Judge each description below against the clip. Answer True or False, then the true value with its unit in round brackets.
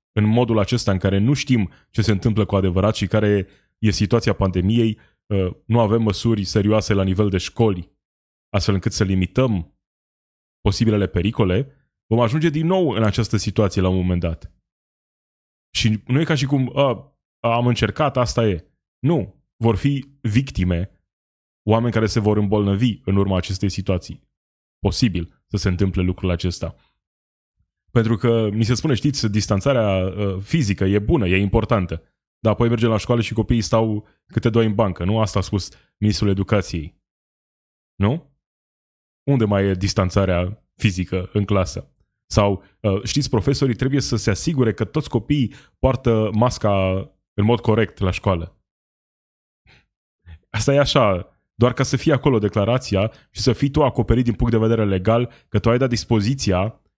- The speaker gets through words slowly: False (160 wpm)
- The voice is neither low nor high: False (105 Hz)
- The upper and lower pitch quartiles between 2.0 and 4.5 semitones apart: True (3.8 semitones)